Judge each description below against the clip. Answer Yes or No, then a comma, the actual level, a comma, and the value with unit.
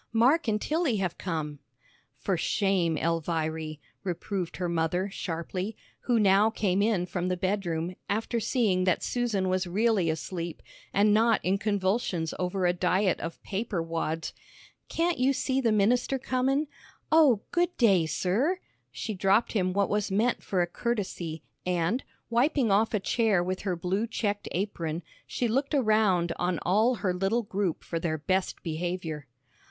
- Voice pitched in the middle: No, high, 195 Hz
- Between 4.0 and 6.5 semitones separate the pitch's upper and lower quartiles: Yes, average, 4.4 semitones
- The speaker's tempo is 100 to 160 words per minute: Yes, average, 155 wpm